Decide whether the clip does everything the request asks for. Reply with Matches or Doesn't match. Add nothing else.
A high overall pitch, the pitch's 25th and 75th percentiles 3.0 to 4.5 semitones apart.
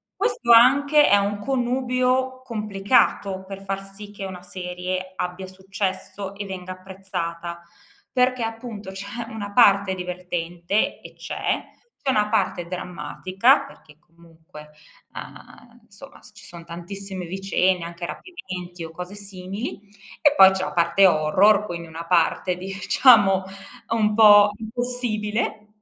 Matches